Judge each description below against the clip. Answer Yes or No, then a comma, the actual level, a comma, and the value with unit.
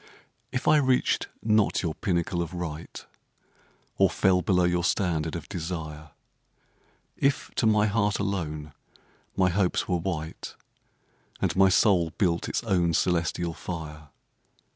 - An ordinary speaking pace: No, slow, 130 wpm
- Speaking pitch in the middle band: No, very low, 90 Hz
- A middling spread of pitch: Yes, average, 3.3 semitones